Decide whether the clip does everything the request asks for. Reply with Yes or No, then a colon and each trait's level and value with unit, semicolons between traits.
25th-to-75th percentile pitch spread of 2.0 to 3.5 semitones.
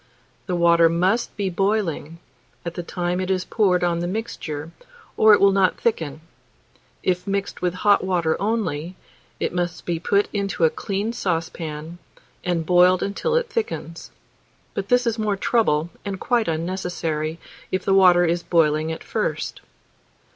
Yes: average, 3.1 semitones